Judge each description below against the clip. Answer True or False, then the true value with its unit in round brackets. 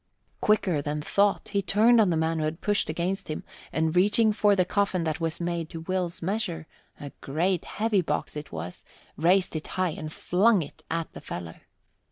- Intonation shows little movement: False (4.0 semitones)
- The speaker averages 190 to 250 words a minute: True (195 wpm)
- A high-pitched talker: False (175 Hz)